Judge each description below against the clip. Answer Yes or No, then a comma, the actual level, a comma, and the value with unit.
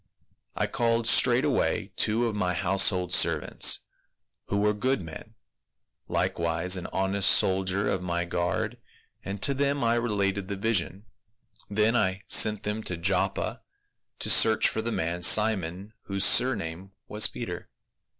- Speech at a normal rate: Yes, average, 150 wpm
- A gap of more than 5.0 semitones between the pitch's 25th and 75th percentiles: No, average, 3.3 semitones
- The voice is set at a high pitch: No, low, 100 Hz